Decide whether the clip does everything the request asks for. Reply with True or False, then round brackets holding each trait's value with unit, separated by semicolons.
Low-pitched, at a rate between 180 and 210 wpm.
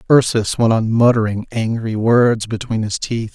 False (115 Hz; 160 wpm)